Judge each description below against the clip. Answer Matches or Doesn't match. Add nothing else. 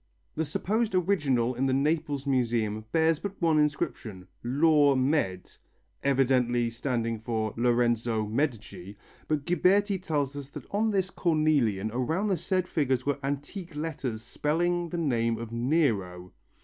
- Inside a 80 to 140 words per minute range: Matches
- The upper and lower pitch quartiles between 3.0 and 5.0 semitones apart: Doesn't match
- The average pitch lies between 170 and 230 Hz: Doesn't match